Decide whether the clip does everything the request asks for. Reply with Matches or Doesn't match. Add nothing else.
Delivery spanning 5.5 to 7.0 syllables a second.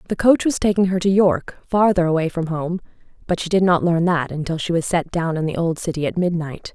Matches